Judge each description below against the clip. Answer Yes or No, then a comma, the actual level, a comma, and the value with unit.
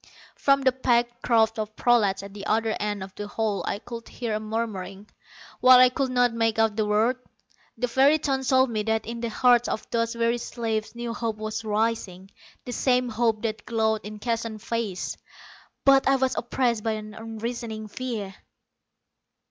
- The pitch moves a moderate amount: No, narrow, 2.1 semitones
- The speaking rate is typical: Yes, average, 180 wpm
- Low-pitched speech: No, high, 225 Hz